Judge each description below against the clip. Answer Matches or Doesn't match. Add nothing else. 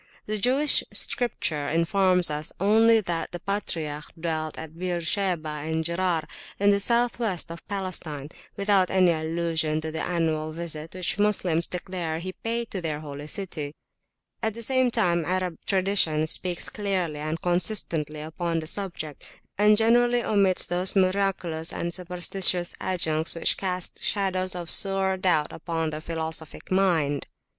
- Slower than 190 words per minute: Matches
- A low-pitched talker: Doesn't match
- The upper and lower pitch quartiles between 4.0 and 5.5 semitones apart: Doesn't match